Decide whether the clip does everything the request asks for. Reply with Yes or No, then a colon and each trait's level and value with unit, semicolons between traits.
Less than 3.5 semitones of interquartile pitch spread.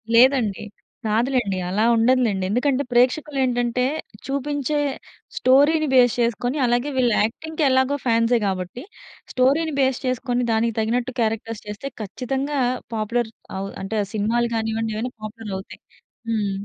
Yes: average, 2.9 semitones